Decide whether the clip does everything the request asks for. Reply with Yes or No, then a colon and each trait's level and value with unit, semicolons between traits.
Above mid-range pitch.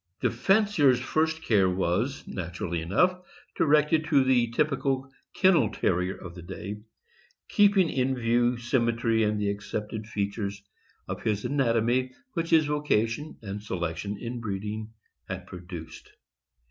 No: low, 115 Hz